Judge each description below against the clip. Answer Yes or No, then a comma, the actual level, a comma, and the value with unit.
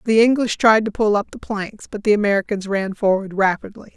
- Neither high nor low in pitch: No, high, 205 Hz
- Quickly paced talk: Yes, fast, 210 wpm